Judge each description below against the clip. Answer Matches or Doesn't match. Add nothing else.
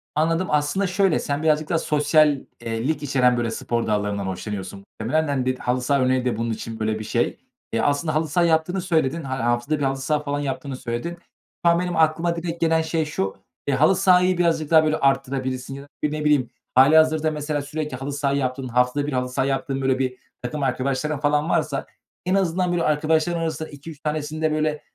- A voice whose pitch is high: Doesn't match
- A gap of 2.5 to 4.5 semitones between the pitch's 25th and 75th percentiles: Matches